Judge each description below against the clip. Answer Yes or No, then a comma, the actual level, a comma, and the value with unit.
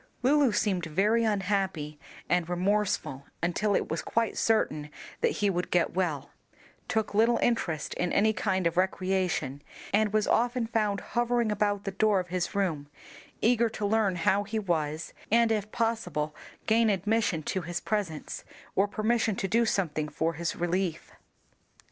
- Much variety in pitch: No, average, 4.1 semitones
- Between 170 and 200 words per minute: No, average, 155 wpm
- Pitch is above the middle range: Yes, high, 195 Hz